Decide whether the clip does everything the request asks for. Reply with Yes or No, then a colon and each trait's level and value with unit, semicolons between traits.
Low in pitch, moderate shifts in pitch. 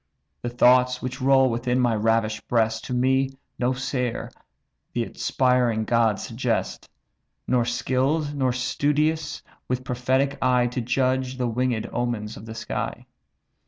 No: low, 125 Hz; narrow, 1.9 semitones